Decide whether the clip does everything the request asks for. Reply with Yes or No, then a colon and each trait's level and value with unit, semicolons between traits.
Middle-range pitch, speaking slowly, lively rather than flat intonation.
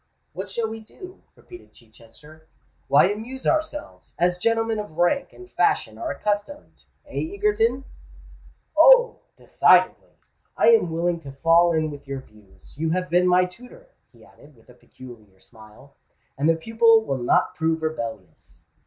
No: medium, 175 Hz; average, 145 wpm; wide, 8.5 semitones